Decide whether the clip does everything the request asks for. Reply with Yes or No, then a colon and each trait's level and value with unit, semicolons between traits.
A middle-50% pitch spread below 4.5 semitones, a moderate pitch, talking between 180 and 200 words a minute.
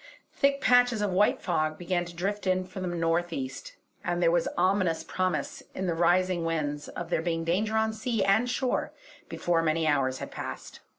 Yes: average, 3.1 semitones; medium, 175 Hz; average, 190 wpm